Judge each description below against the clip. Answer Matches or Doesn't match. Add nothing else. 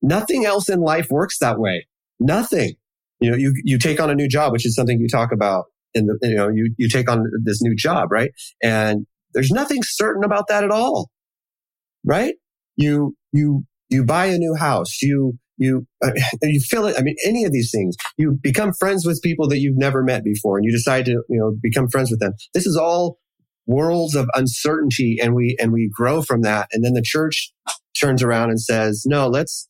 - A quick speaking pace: Matches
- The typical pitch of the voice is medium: Doesn't match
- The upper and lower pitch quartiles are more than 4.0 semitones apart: Matches